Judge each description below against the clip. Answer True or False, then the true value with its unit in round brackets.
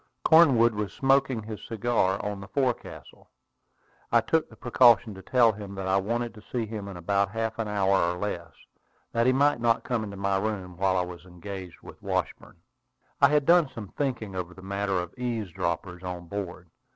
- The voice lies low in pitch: True (105 Hz)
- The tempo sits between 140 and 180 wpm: False (190 wpm)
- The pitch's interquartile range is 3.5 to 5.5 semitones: True (3.8 semitones)